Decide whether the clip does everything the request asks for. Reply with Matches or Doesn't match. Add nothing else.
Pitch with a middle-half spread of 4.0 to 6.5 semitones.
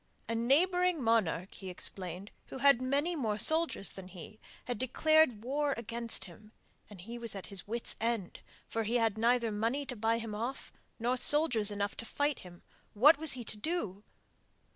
Matches